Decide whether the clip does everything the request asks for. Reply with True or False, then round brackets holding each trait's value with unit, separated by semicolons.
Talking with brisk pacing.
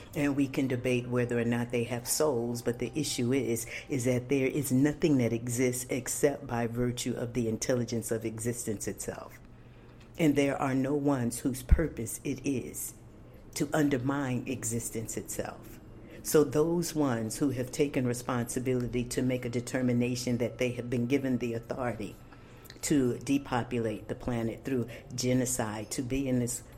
False (160 wpm)